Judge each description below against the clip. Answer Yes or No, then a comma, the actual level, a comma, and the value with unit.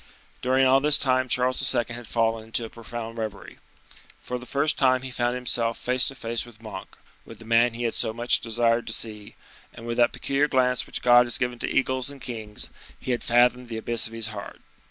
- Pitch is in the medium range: No, low, 120 Hz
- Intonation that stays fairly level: Yes, narrow, 1.8 semitones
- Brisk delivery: Yes, fast, 220 wpm